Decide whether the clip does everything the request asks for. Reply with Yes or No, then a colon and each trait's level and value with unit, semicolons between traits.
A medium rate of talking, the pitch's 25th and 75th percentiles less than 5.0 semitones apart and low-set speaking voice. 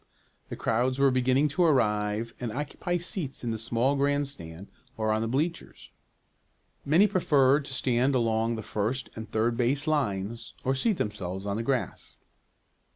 Yes: average, 155 wpm; average, 4.2 semitones; low, 125 Hz